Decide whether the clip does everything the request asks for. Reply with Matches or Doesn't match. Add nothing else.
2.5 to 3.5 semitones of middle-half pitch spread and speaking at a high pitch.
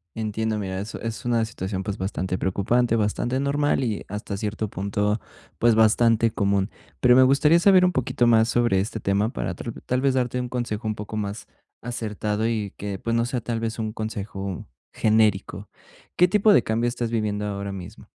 Doesn't match